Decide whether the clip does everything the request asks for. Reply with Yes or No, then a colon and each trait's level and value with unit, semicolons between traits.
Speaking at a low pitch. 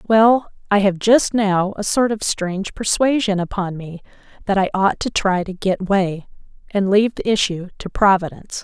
No: high, 200 Hz